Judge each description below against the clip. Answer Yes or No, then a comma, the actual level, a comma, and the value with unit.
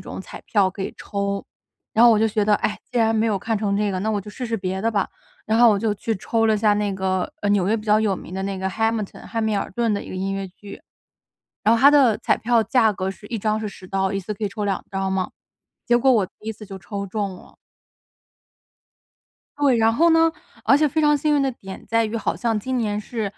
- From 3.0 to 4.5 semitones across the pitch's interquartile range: No, narrow, 2.5 semitones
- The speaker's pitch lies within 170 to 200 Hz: No, high, 210 Hz